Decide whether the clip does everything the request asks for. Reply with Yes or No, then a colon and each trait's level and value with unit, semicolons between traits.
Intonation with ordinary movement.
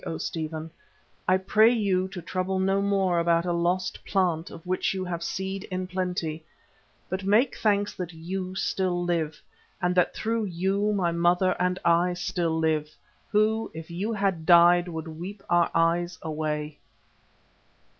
No: narrow, 2.2 semitones